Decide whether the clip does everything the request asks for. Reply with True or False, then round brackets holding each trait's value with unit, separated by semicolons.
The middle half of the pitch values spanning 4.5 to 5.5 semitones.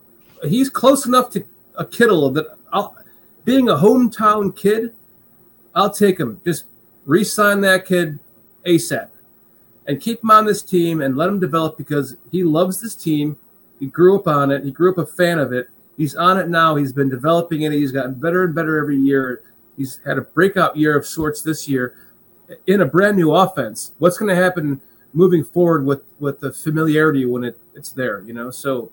True (5.1 semitones)